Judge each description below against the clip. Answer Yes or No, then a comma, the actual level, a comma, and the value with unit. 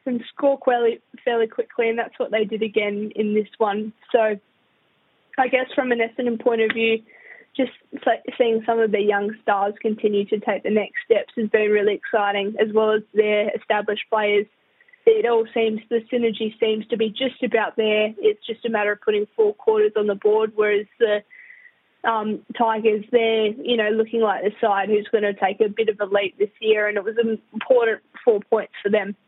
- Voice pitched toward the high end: Yes, high, 220 Hz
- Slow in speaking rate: No, fast, 205 wpm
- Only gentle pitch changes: Yes, narrow, 2.3 semitones